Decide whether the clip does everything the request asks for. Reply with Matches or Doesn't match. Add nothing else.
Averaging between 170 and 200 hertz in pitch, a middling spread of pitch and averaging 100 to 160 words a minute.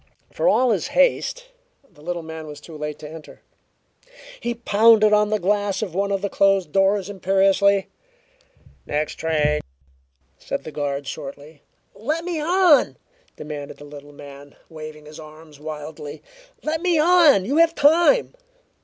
Doesn't match